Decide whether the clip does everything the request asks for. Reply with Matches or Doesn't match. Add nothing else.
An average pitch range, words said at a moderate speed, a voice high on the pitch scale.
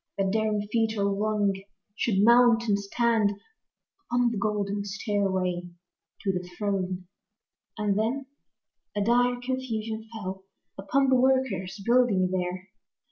Doesn't match